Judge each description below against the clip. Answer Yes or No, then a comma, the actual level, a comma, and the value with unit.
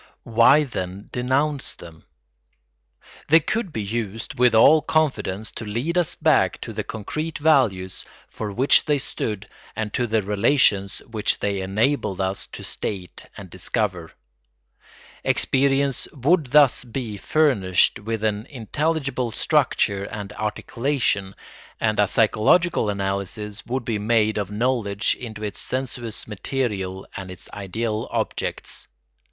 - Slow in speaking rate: Yes, slow, 130 wpm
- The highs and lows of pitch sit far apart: No, average, 4.8 semitones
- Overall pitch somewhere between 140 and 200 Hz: No, low, 110 Hz